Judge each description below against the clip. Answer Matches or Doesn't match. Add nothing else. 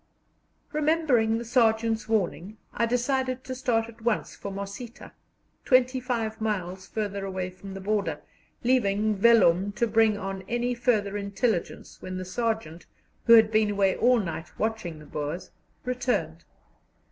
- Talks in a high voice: Matches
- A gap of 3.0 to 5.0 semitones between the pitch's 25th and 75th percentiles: Matches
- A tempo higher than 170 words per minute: Doesn't match